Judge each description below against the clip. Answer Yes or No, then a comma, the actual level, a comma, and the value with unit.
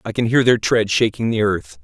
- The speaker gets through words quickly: Yes, fast, 260 wpm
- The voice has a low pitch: Yes, low, 110 Hz